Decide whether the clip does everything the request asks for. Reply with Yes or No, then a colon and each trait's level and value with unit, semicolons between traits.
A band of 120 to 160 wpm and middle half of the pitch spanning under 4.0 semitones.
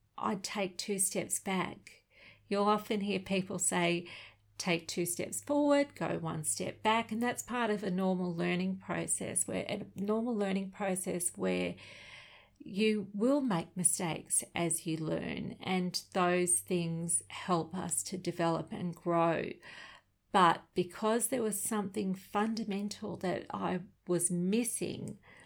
Yes: slow, 135 wpm; average, 3.2 semitones